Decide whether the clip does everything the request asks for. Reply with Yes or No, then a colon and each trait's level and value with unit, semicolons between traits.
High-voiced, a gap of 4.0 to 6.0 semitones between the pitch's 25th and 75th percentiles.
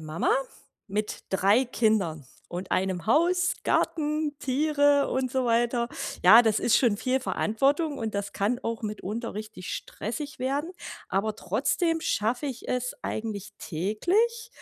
Yes: high, 235 Hz; wide, 5.5 semitones